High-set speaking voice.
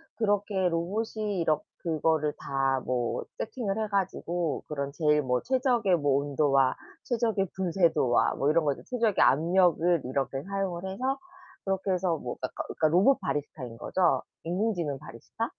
No: medium, 170 Hz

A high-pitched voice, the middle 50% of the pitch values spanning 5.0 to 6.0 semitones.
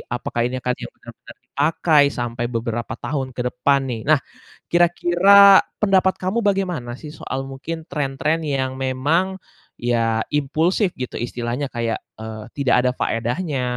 No: low, 135 Hz; wide, 5.5 semitones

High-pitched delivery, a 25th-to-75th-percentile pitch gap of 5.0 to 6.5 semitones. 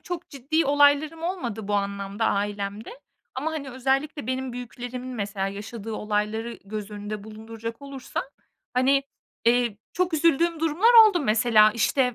Yes: high, 245 Hz; average, 5.3 semitones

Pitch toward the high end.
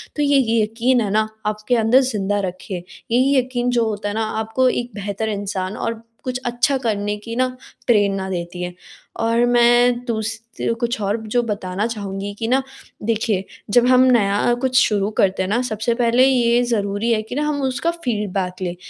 Yes: high, 225 Hz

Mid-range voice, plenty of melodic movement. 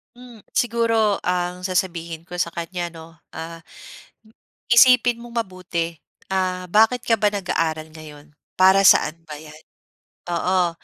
No: medium, 180 Hz; average, 4.0 semitones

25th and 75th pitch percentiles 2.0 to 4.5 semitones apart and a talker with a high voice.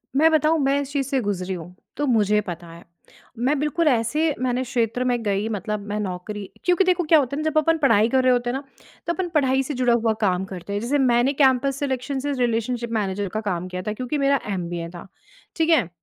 No: wide, 5.6 semitones; high, 245 Hz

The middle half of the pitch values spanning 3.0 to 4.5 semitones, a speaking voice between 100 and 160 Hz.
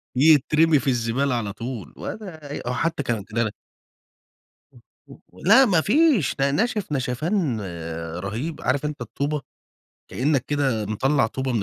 No: average, 5.0 semitones; medium, 140 Hz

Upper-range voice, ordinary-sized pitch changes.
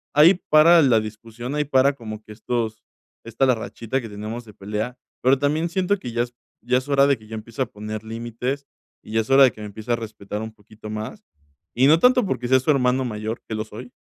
No: low, 120 Hz; average, 3.8 semitones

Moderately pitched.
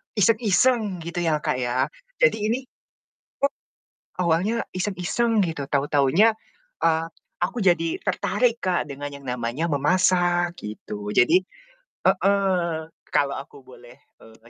Yes: medium, 170 Hz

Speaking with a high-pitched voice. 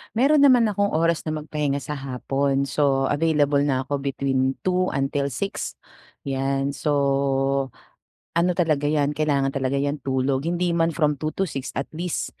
No: medium, 145 Hz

